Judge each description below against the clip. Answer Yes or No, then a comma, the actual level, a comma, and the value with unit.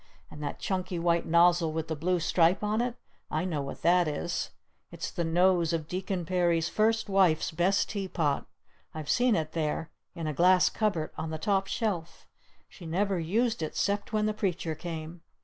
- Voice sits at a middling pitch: Yes, medium, 175 Hz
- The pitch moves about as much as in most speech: Yes, average, 3.2 semitones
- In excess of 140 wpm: Yes, average, 185 wpm